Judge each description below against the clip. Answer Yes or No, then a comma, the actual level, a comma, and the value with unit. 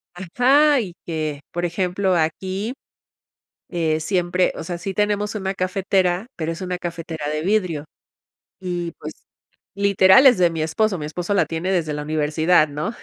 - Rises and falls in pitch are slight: No, average, 3.3 semitones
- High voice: No, medium, 180 Hz